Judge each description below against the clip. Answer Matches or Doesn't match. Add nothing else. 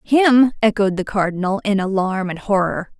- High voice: Matches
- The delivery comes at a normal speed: Matches